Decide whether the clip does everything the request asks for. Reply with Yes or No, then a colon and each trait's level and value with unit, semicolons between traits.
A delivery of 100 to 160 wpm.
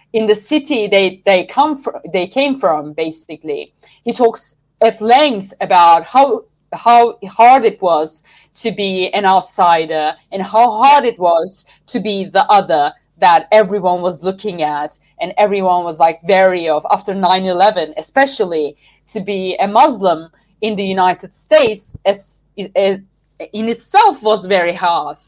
Yes: average, 150 wpm